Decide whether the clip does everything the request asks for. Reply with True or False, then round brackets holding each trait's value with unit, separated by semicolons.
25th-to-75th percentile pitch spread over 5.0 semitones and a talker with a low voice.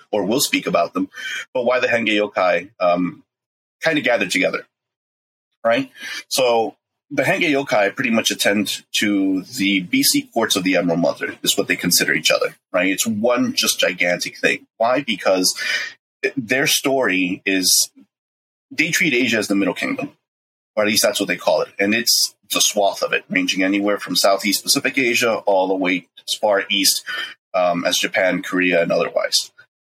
True (5.4 semitones; 100 Hz)